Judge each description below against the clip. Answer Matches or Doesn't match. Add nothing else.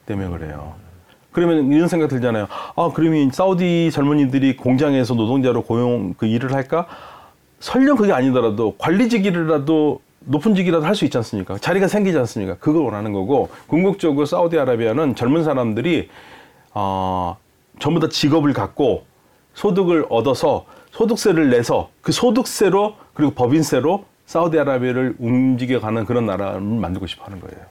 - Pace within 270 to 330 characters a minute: Doesn't match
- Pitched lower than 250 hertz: Matches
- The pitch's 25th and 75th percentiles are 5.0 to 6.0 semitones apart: Doesn't match